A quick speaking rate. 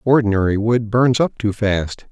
No: average, 170 wpm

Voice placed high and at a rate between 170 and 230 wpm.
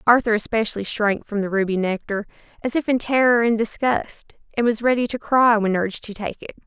Yes: high, 220 Hz; fast, 205 wpm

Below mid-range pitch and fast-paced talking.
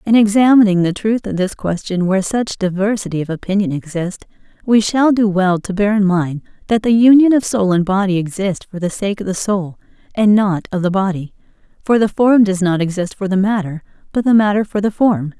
No: high, 200 Hz; fast, 215 wpm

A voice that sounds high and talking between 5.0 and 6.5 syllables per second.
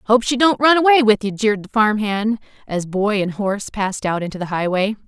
Yes: high, 215 Hz; 5.6 syllables/s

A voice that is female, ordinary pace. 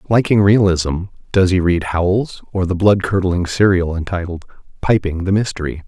No: male; average, 155 wpm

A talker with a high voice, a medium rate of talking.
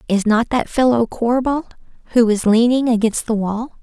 Yes: high, 235 Hz; average, 175 wpm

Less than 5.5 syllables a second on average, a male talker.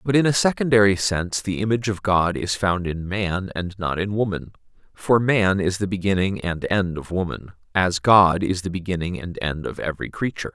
Yes: 5.3 syllables/s; male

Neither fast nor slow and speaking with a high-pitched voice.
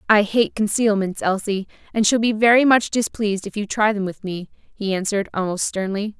Yes: average, 195 wpm; high, 205 Hz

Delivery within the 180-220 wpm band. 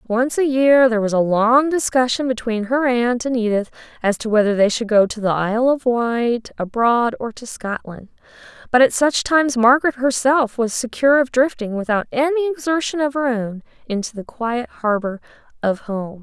Yes: average, 185 wpm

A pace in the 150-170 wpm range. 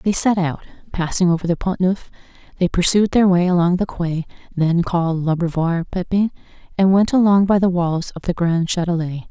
No: average, 185 wpm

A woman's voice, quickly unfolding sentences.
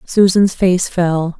No: female; slow, 130 wpm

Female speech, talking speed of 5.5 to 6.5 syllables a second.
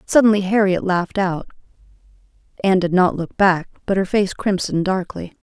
Yes: female; 5.6 syllables/s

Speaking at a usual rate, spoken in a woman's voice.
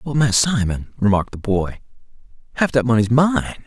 No: average, 165 wpm; male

